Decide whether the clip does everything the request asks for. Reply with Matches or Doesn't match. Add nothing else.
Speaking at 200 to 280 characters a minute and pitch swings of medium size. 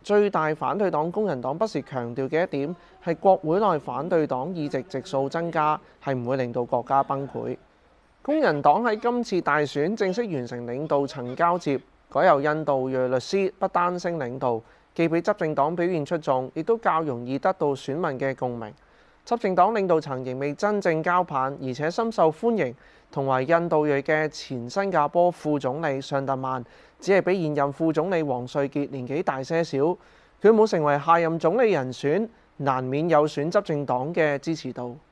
Matches